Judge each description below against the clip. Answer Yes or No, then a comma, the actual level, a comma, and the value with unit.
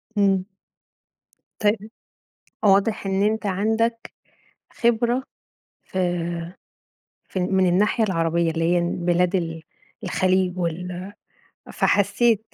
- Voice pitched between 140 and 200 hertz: Yes, high, 190 Hz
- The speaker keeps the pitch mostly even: No, average, 3.1 semitones